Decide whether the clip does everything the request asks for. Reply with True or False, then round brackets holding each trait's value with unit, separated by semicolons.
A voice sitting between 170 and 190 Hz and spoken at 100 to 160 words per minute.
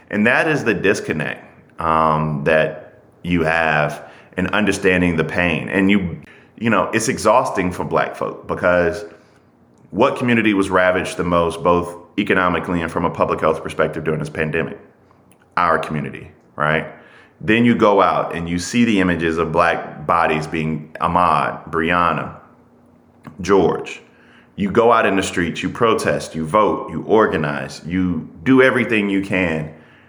False (85 Hz; 150 wpm)